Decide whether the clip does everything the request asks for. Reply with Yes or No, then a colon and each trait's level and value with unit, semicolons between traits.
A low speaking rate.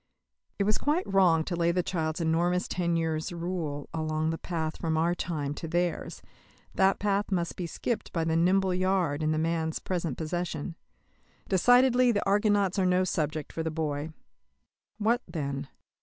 No: average, 170 wpm